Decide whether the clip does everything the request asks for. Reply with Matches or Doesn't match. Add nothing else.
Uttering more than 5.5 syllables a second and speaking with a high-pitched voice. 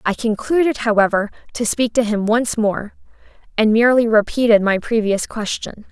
Doesn't match